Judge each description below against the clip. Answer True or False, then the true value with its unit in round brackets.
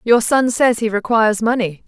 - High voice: True (225 Hz)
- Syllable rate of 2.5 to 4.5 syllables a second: False (5.1 syllables/s)